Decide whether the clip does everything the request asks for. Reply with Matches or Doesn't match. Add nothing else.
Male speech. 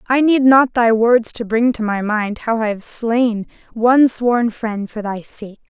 Doesn't match